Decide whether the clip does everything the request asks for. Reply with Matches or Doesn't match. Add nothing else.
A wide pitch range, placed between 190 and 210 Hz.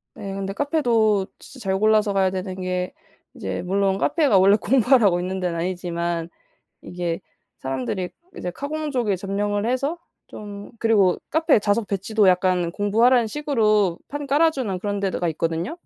Doesn't match